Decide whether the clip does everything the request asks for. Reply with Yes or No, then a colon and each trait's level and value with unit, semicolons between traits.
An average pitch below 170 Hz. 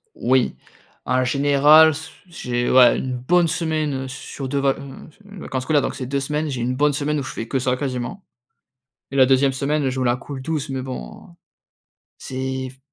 Yes: low, 135 Hz